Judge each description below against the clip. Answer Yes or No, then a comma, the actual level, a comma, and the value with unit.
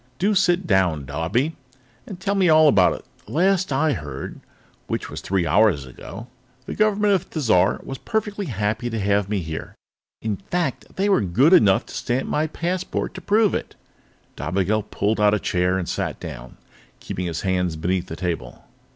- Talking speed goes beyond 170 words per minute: Yes, average, 180 wpm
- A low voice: Yes, low, 110 Hz